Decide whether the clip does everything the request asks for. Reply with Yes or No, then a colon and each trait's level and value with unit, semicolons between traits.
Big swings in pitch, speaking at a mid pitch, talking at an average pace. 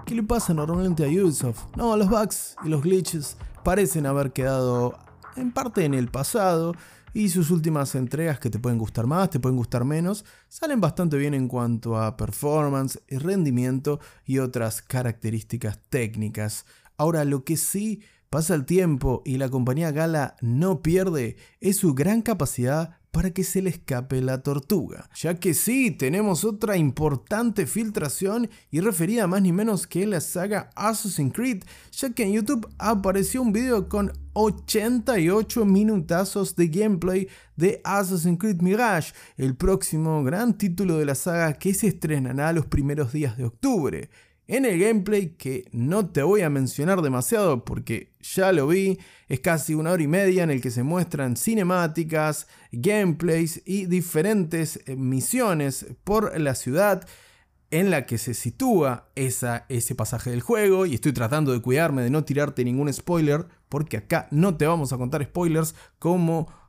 Yes: wide, 6.5 semitones; medium, 165 Hz; average, 160 wpm